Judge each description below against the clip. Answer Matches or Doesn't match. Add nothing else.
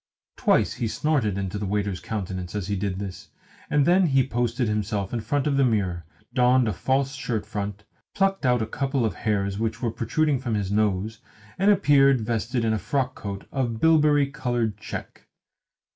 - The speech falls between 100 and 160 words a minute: Doesn't match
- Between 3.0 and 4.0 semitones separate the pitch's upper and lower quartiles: Doesn't match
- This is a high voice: Doesn't match